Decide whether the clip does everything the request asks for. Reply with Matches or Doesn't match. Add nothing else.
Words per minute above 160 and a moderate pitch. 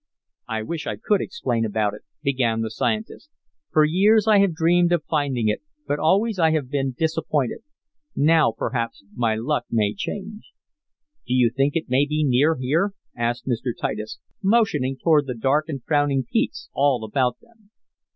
Matches